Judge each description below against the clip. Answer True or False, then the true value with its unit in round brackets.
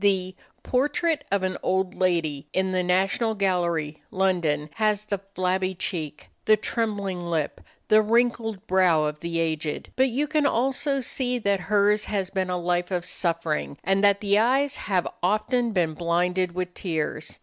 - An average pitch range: True (3.8 semitones)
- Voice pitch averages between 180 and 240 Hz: True (190 Hz)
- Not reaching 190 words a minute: True (160 wpm)